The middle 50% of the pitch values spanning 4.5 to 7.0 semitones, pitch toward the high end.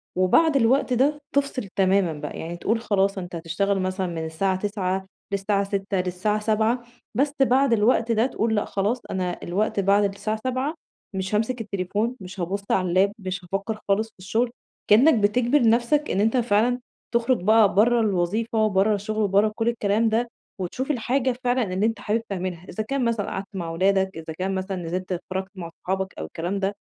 No: average, 3.5 semitones; high, 205 Hz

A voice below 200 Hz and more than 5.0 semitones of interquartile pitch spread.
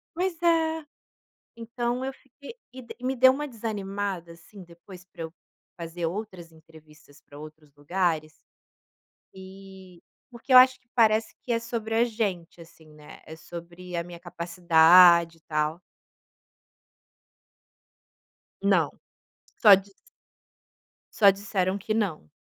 Yes: high, 190 Hz; wide, 5.4 semitones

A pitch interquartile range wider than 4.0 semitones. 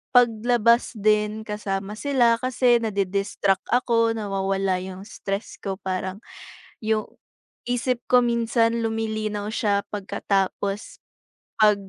No: average, 2.9 semitones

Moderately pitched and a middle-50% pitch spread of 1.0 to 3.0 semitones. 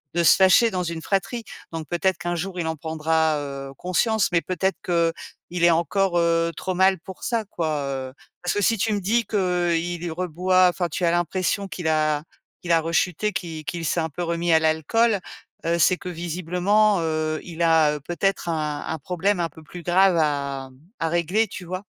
Yes: medium, 175 Hz; narrow, 2.6 semitones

